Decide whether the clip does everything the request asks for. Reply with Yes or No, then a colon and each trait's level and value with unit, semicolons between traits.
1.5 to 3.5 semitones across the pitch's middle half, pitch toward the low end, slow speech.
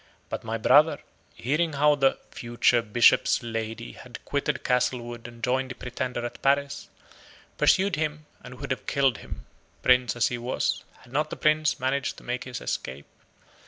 No: average, 2.9 semitones; low, 125 Hz; average, 165 wpm